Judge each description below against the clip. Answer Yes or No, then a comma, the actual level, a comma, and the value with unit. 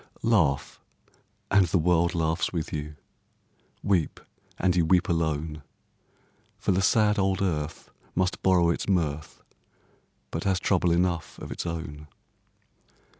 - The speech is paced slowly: Yes, slow, 125 wpm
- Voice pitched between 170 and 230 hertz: No, very low, 85 Hz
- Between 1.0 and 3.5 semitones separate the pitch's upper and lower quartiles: Yes, average, 2.9 semitones